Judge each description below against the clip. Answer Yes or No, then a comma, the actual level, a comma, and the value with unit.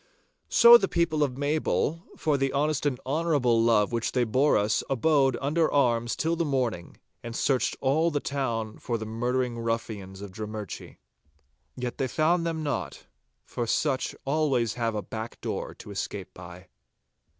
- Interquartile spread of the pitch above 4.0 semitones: Yes, average, 4.8 semitones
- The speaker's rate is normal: Yes, average, 160 wpm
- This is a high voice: No, low, 125 Hz